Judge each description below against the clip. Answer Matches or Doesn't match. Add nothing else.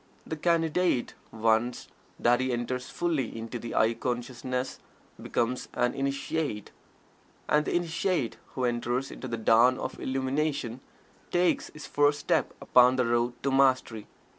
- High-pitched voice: Doesn't match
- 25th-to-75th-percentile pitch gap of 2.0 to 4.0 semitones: Matches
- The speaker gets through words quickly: Doesn't match